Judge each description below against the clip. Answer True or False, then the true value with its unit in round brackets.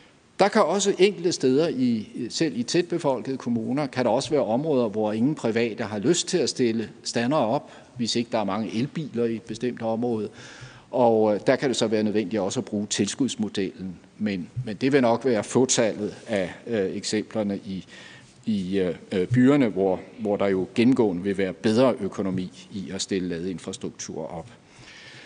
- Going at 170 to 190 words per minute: True (180 wpm)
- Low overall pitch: True (115 Hz)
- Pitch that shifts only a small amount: False (4.2 semitones)